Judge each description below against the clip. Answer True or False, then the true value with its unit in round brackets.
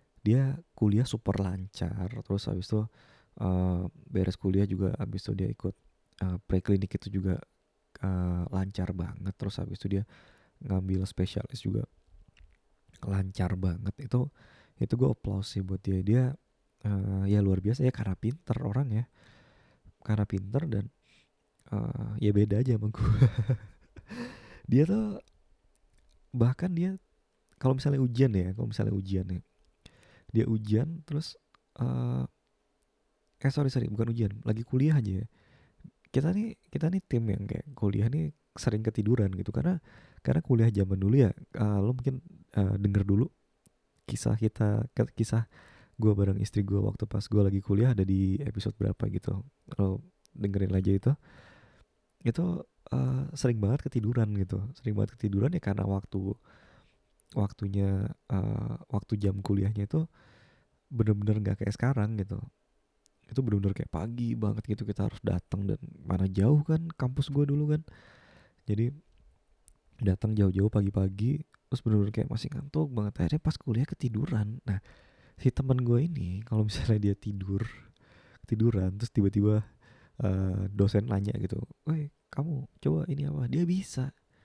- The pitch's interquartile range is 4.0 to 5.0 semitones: True (4.6 semitones)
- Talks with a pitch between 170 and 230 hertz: False (105 Hz)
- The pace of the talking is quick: True (145 wpm)